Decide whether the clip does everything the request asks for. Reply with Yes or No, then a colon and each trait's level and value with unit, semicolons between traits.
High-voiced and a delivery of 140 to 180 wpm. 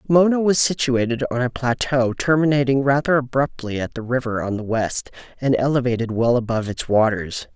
No: low, 125 Hz; average, 165 wpm